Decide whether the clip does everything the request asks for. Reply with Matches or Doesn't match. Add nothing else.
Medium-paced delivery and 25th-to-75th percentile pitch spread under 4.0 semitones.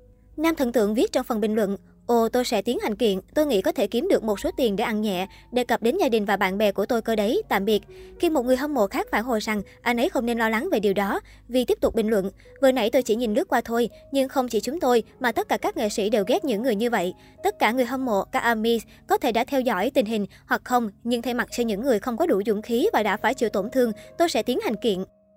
Doesn't match